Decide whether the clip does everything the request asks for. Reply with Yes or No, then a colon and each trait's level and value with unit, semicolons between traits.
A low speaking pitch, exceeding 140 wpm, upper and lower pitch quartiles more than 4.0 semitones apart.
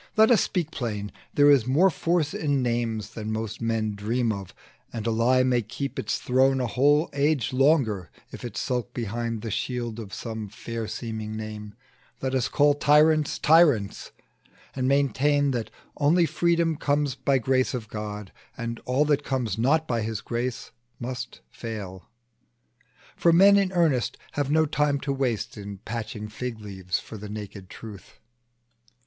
Yes: low, 125 Hz; average, 165 wpm; average, 4.7 semitones